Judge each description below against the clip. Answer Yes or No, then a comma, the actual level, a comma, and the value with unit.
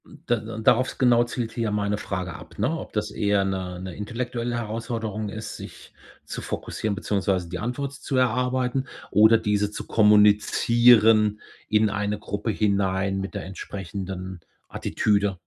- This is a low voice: Yes, low, 105 Hz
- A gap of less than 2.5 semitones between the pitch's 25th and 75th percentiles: No, average, 2.8 semitones